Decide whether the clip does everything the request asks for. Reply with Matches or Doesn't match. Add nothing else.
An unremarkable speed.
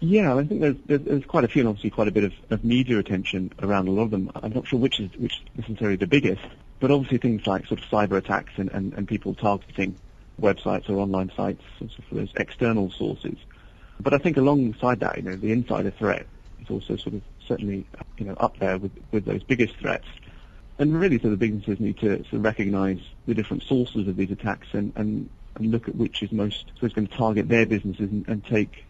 Doesn't match